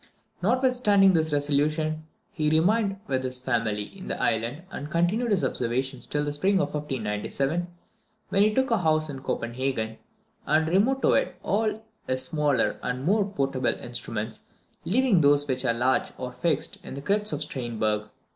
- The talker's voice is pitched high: No, medium, 150 Hz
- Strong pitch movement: Yes, wide, 7.0 semitones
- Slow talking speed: No, average, 165 wpm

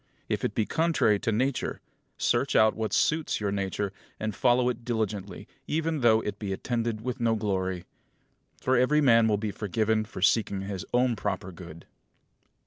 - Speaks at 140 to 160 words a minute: No, average, 170 wpm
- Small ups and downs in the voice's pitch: No, average, 3.5 semitones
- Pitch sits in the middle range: No, low, 110 Hz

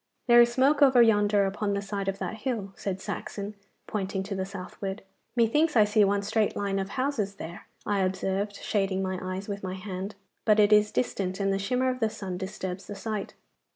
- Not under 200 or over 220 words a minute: Yes, fast, 205 wpm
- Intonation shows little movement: Yes, narrow, 2.2 semitones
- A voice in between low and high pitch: No, high, 200 Hz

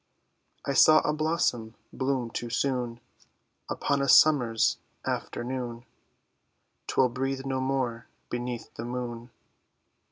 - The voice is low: Yes, low, 125 Hz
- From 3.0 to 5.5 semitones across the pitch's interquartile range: No, narrow, 2.4 semitones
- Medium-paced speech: No, slow, 105 wpm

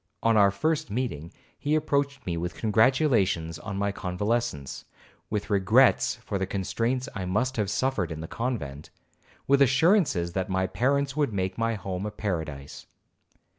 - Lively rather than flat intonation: Yes, wide, 6.0 semitones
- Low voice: Yes, low, 105 Hz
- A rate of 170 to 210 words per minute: No, average, 155 wpm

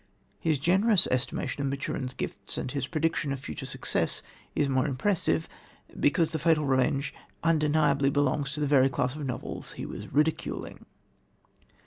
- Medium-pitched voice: Yes, medium, 145 Hz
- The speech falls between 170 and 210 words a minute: No, average, 155 wpm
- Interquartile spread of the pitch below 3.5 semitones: Yes, average, 2.8 semitones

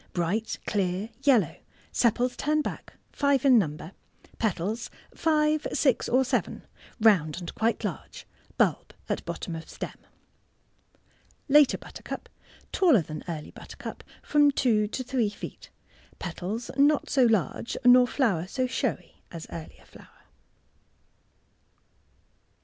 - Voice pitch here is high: Yes, high, 230 Hz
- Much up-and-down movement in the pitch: Yes, wide, 6.8 semitones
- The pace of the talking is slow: Yes, slow, 125 wpm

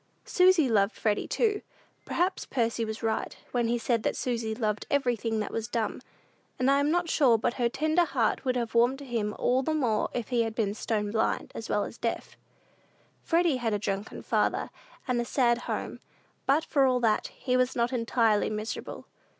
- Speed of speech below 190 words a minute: No, average, 195 wpm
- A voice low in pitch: No, high, 240 Hz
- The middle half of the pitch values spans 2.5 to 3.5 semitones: Yes, average, 3.2 semitones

